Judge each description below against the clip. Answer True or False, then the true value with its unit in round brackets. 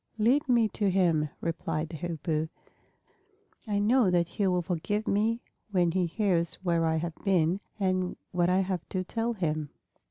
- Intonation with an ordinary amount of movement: True (3.6 semitones)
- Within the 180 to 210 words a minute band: False (165 wpm)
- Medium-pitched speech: True (180 Hz)